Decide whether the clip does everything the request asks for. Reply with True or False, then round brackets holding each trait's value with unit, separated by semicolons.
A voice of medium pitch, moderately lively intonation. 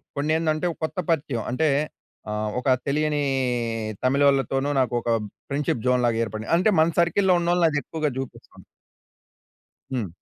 True (145 Hz; 3.9 semitones)